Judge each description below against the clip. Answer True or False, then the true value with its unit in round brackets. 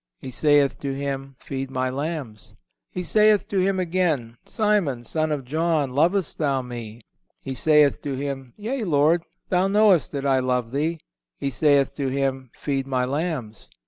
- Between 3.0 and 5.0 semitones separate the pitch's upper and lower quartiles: True (4.0 semitones)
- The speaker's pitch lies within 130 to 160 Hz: True (140 Hz)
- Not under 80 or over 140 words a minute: False (165 wpm)